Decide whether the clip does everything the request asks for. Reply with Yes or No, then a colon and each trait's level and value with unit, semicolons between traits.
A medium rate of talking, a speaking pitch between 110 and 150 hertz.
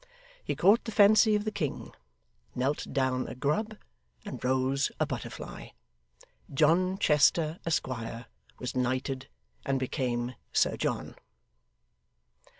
No: slow, 115 wpm; medium, 140 Hz